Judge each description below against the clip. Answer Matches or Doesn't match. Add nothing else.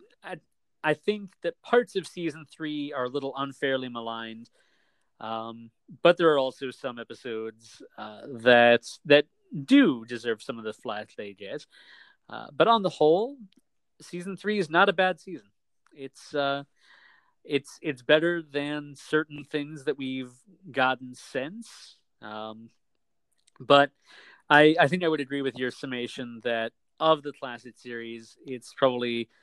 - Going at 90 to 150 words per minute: Matches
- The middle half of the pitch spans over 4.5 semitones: Matches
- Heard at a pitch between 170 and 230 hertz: Doesn't match